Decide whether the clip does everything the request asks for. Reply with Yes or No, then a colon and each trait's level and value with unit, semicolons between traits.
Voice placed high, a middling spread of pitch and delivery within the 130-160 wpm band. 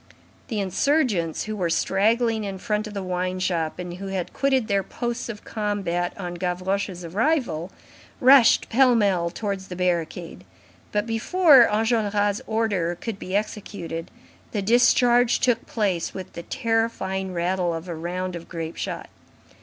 Yes: high, 200 Hz; average, 4.1 semitones; average, 150 wpm